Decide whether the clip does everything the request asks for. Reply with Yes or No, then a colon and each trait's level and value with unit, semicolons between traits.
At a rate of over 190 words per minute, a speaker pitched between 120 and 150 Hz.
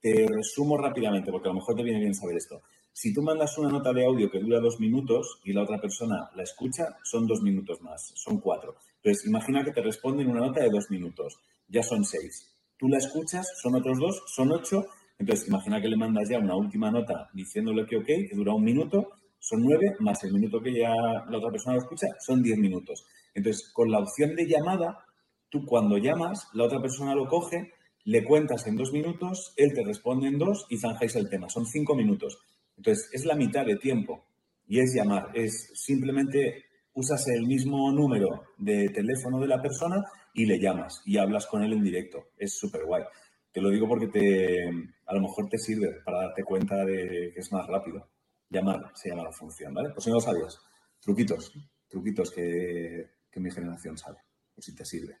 Yes: fast, 205 wpm; low, 135 Hz